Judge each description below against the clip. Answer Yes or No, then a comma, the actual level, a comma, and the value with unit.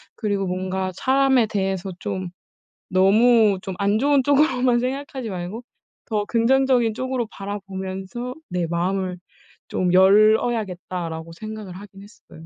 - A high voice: Yes, high, 205 Hz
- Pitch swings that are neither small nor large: Yes, average, 4.3 semitones